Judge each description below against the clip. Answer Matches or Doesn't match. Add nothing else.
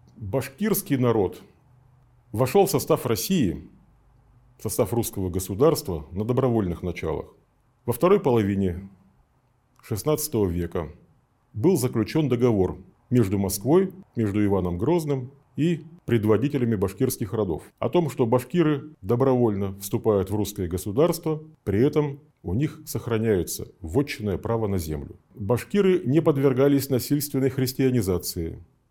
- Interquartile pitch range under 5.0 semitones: Doesn't match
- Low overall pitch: Matches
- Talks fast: Doesn't match